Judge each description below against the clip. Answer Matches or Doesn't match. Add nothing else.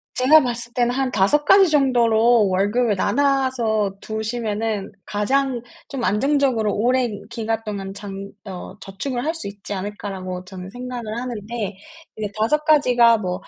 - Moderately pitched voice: Doesn't match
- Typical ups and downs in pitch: Matches